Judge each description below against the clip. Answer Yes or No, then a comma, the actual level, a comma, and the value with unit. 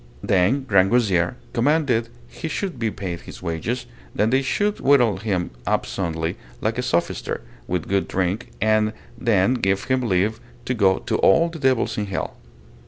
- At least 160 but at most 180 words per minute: Yes, average, 165 wpm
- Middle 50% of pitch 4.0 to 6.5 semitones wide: Yes, average, 5.0 semitones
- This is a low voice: Yes, low, 110 Hz